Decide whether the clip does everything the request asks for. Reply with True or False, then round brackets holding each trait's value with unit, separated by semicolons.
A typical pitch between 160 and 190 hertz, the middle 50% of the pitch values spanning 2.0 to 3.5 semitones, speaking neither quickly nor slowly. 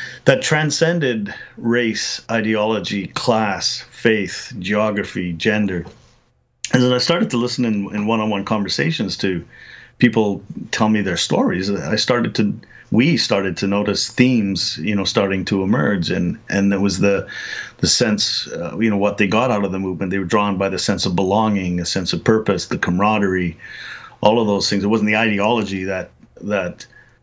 False (105 Hz; 2.5 semitones; 170 wpm)